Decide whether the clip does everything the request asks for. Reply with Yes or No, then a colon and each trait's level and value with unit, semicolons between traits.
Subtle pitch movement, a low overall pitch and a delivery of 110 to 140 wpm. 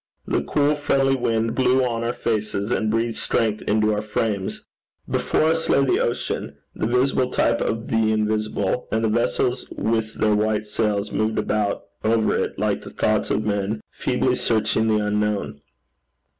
No: narrow, 2.2 semitones; low, 110 Hz; average, 165 wpm